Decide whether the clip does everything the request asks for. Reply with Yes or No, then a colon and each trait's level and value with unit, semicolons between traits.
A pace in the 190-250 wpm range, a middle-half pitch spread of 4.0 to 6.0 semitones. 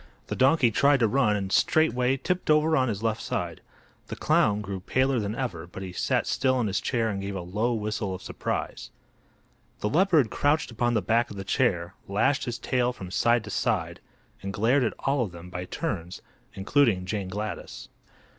Yes: average, 195 wpm; average, 5.0 semitones